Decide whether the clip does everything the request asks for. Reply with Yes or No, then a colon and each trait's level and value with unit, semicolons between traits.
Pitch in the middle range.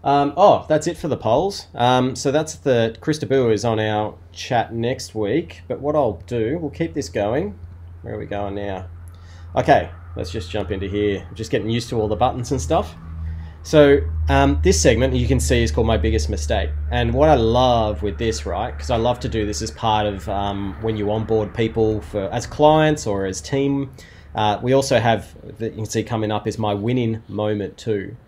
No: low, 110 Hz